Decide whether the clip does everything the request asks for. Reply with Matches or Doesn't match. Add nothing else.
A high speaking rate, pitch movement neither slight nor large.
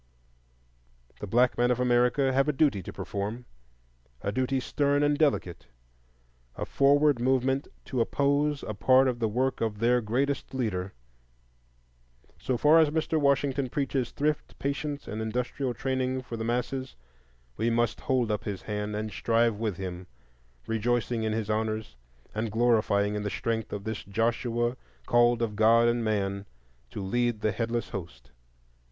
Doesn't match